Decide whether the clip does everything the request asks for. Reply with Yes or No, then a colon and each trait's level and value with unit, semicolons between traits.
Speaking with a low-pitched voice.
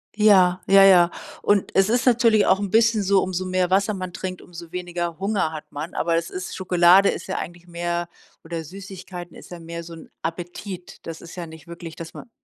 No: medium, 180 Hz